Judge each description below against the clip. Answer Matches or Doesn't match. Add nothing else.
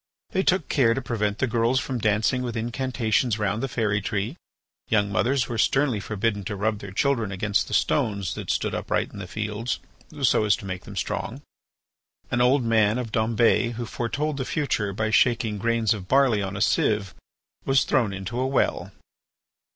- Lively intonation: Doesn't match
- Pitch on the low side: Matches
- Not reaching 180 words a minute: Doesn't match